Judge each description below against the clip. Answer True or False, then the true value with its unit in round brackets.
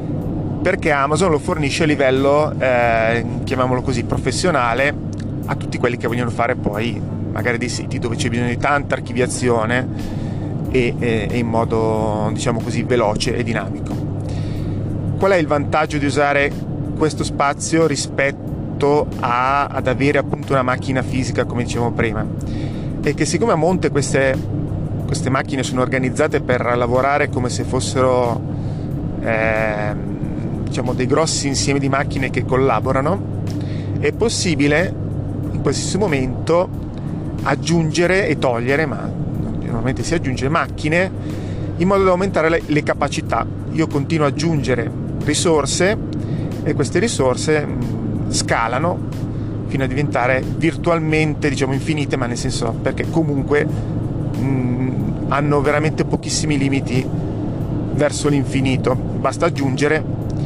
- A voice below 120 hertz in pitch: False (135 Hz)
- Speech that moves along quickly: False (125 wpm)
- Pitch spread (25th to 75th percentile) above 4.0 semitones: False (3.5 semitones)